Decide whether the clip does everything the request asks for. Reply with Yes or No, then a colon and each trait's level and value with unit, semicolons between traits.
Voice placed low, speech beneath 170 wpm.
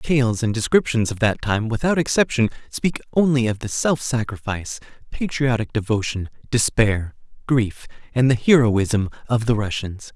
Yes: low, 120 Hz; average, 150 wpm